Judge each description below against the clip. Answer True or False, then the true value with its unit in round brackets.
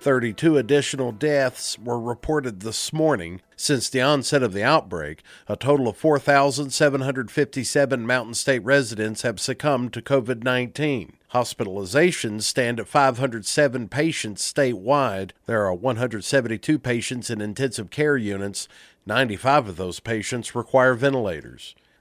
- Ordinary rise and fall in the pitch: True (3.9 semitones)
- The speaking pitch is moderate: False (130 Hz)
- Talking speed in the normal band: False (125 wpm)